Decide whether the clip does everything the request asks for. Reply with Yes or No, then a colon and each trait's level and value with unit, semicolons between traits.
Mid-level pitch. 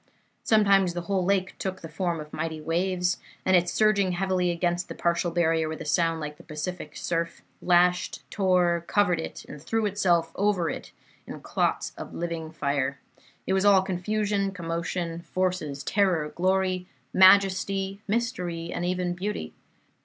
Yes: medium, 180 Hz